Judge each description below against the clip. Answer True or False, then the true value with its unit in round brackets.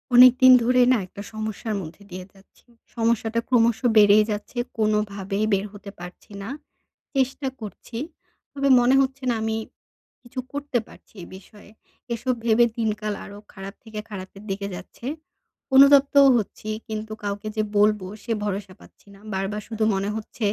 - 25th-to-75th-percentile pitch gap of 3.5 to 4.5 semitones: False (3.1 semitones)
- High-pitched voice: True (215 Hz)